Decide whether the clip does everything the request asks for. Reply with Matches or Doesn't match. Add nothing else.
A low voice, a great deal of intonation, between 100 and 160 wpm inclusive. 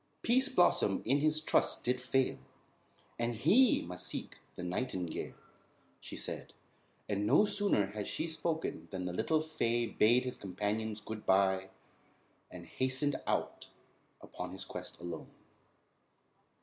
Matches